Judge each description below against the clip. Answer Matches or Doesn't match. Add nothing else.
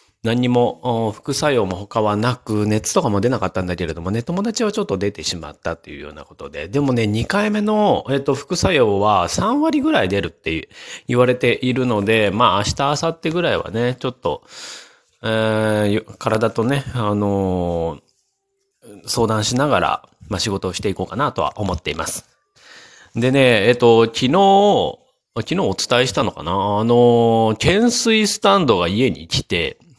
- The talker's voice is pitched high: Doesn't match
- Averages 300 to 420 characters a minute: Matches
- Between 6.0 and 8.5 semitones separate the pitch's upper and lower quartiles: Doesn't match